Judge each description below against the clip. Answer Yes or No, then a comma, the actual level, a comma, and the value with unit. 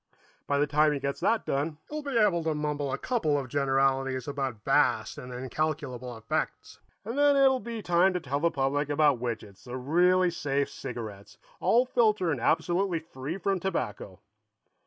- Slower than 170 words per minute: No, average, 175 wpm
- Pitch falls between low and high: Yes, medium, 145 Hz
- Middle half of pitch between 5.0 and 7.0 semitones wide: Yes, average, 5.3 semitones